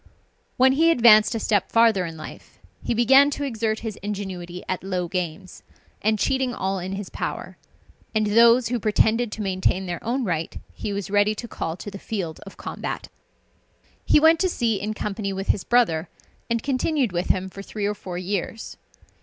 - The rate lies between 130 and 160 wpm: No, average, 185 wpm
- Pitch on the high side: Yes, high, 210 Hz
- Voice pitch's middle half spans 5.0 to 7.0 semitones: No, average, 3.7 semitones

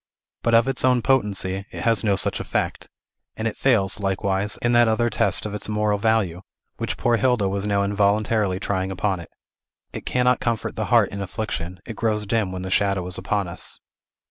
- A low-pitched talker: Yes, low, 105 Hz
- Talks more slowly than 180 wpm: No, average, 195 wpm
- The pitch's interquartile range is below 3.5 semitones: Yes, average, 2.9 semitones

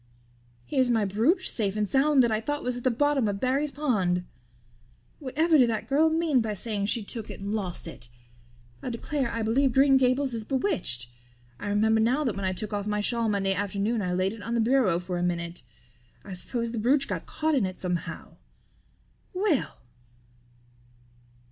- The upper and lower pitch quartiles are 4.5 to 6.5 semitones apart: Yes, average, 5.1 semitones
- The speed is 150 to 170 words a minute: No, average, 190 wpm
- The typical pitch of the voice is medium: No, high, 230 Hz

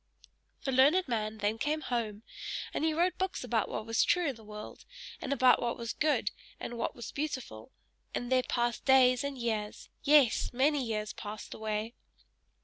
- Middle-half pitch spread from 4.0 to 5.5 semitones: Yes, average, 4.4 semitones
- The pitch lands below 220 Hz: No, high, 245 Hz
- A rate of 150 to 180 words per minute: Yes, average, 175 wpm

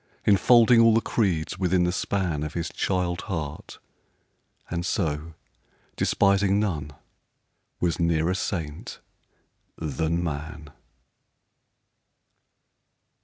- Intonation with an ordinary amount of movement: Yes, average, 3.7 semitones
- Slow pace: Yes, slow, 90 wpm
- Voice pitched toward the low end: Yes, very low, 85 Hz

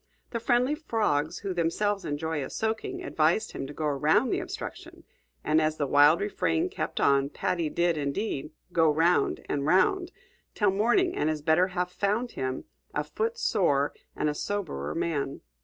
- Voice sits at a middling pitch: Yes, medium, 165 Hz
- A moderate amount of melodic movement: No, wide, 5.9 semitones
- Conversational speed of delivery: Yes, average, 170 wpm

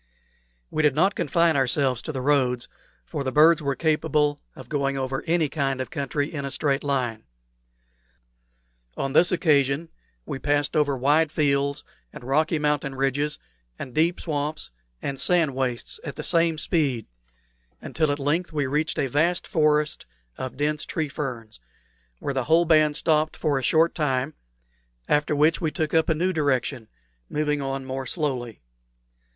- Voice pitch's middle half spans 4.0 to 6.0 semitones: No, narrow, 2.6 semitones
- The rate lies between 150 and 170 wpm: Yes, average, 160 wpm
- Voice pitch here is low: No, medium, 145 Hz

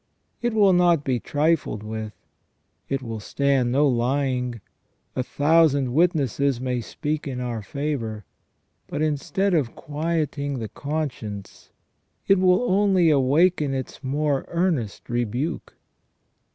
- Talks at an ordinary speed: No, slow, 125 wpm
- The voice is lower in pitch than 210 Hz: Yes, medium, 140 Hz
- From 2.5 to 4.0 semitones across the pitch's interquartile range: No, average, 4.5 semitones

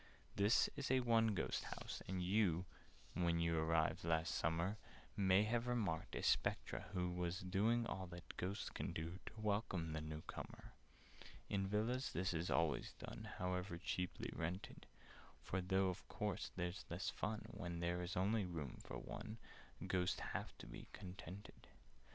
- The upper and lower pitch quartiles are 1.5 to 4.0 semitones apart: Yes, average, 3.2 semitones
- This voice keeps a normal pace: Yes, average, 165 wpm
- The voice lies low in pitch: Yes, very low, 90 Hz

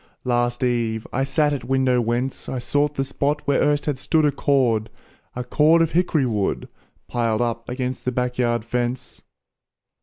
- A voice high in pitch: No, low, 125 Hz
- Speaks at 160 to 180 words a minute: Yes, average, 175 wpm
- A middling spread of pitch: Yes, average, 3.0 semitones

